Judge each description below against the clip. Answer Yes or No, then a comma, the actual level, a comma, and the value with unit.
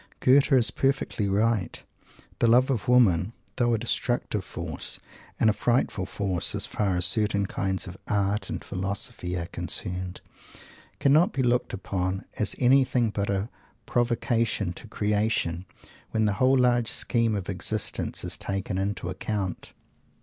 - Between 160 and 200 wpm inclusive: No, average, 145 wpm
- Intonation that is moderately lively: Yes, average, 3.9 semitones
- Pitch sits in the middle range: No, low, 105 Hz